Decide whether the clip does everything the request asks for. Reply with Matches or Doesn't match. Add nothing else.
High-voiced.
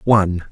Doesn't match